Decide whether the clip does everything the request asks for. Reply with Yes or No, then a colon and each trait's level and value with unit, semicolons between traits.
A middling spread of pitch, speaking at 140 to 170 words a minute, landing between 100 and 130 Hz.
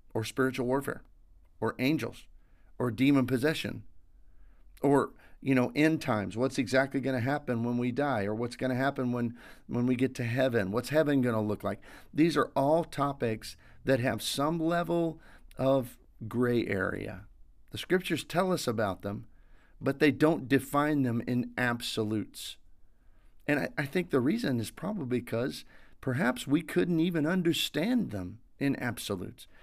Yes: average, 4.6 semitones; average, 155 wpm; low, 125 Hz